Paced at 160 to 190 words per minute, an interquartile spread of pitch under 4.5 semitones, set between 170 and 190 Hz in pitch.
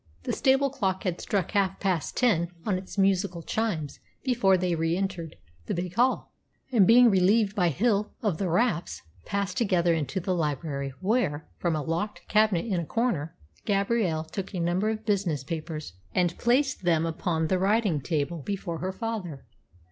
Yes: average, 170 wpm; average, 4.1 semitones; medium, 185 Hz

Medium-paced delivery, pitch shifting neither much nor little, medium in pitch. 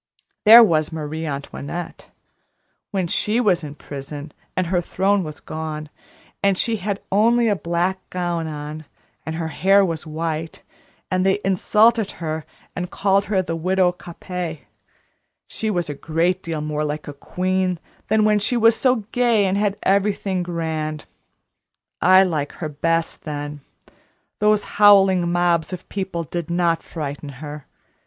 Yes: average, 150 wpm; average, 3.9 semitones; medium, 175 Hz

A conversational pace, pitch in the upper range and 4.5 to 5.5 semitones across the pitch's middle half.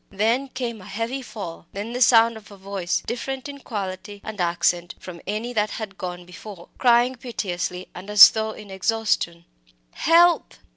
No: average, 165 wpm; high, 210 Hz; average, 4.1 semitones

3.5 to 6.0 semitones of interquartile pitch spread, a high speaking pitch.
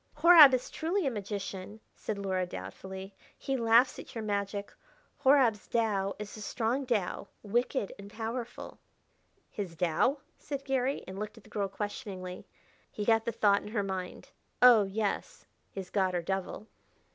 Yes: average, 3.8 semitones; high, 210 Hz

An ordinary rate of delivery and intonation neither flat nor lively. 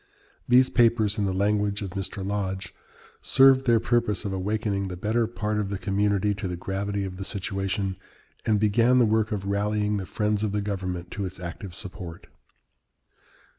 No: average, 175 wpm; narrow, 1.8 semitones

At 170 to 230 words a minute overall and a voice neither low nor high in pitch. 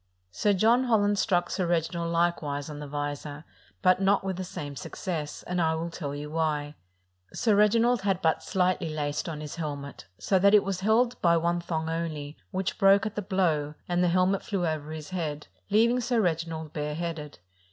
Yes: average, 195 wpm; medium, 170 Hz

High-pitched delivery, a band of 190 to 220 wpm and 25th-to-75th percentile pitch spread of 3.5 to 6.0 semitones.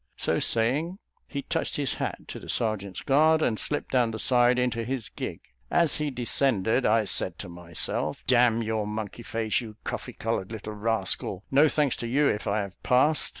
No: low, 115 Hz; average, 195 wpm; average, 3.9 semitones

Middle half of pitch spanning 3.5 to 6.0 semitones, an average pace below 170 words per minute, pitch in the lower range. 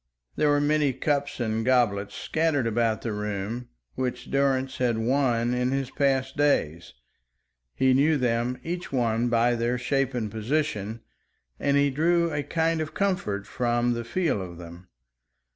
Yes: average, 3.8 semitones; average, 155 wpm; low, 125 Hz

